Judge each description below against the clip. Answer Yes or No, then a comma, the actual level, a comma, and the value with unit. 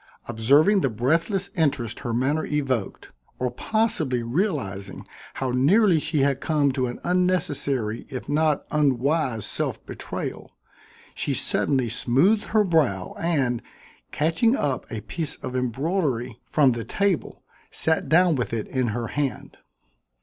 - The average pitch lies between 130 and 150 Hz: Yes, medium, 140 Hz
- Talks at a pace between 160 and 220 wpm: No, slow, 135 wpm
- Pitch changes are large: No, average, 5.0 semitones